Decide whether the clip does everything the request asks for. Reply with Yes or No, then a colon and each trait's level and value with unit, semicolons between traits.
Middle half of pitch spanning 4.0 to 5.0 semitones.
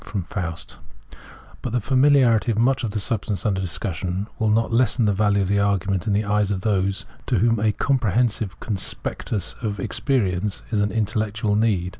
No: average, 2.7 semitones